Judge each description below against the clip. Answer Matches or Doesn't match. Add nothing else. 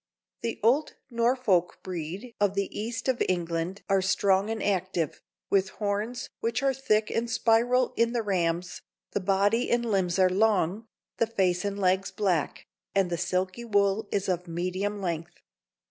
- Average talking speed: Matches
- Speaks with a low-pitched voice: Doesn't match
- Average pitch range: Matches